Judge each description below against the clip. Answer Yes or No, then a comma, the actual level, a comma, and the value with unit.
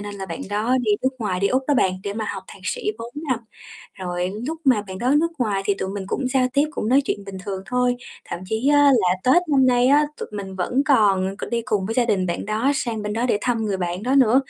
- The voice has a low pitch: No, high, 220 Hz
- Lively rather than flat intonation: No, average, 4.7 semitones